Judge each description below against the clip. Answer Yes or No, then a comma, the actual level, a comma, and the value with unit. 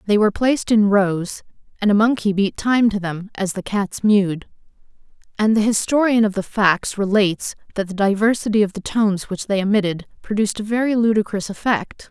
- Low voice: No, high, 205 Hz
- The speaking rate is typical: Yes, average, 185 wpm